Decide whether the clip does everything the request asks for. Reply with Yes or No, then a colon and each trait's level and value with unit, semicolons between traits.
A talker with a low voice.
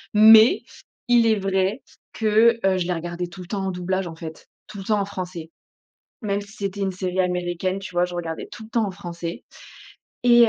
No: high, 190 Hz